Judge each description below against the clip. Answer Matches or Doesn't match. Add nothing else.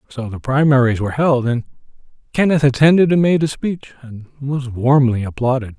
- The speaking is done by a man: Matches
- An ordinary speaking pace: Matches